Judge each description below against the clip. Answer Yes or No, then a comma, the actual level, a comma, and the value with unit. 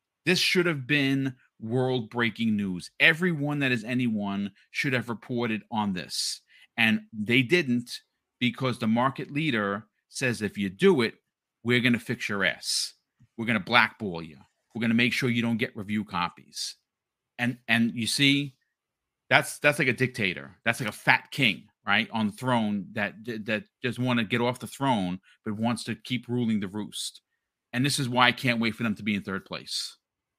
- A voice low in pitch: Yes, low, 120 Hz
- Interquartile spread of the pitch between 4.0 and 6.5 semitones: No, average, 3.0 semitones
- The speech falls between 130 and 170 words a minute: No, average, 185 wpm